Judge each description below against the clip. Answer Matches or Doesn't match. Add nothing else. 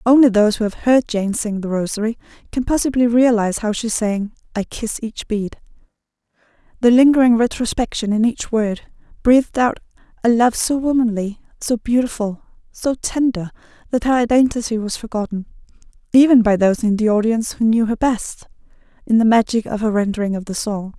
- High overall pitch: Matches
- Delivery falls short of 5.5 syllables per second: Doesn't match